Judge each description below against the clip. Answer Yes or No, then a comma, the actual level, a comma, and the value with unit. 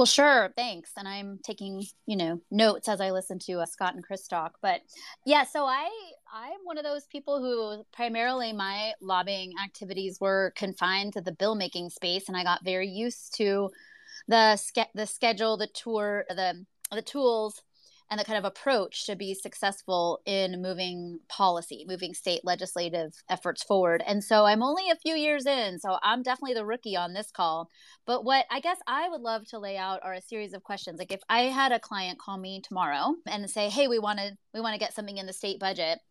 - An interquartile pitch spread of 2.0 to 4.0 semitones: Yes, average, 3.7 semitones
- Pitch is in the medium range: No, high, 205 Hz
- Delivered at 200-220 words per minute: Yes, fast, 205 wpm